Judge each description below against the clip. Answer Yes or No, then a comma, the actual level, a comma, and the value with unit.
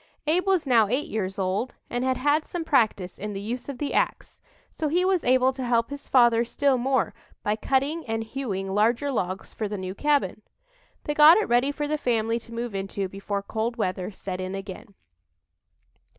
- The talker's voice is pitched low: No, high, 235 Hz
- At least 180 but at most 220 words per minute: Yes, average, 195 wpm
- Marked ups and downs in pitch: Yes, wide, 5.8 semitones